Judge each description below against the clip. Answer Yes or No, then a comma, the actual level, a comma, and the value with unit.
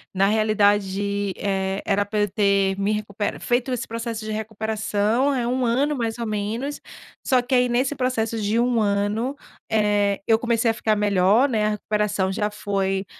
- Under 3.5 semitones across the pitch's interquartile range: Yes, narrow, 2.6 semitones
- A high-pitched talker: Yes, high, 215 Hz